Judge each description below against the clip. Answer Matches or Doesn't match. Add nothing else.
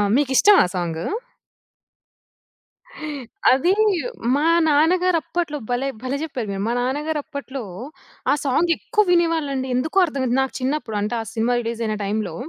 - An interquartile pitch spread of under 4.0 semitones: Doesn't match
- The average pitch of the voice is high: Matches